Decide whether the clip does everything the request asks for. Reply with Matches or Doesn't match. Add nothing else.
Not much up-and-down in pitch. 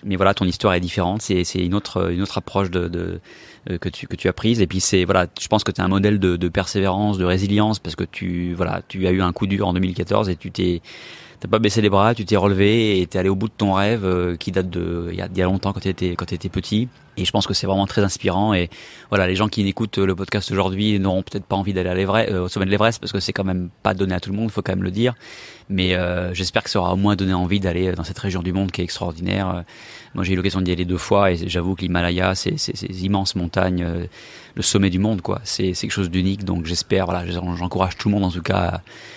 Matches